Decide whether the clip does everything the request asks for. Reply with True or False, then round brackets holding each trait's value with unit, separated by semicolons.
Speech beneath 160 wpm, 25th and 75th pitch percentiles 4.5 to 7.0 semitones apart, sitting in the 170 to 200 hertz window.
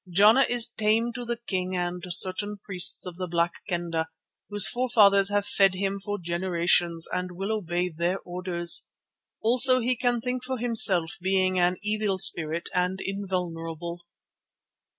False (150 wpm; 3.4 semitones; 190 Hz)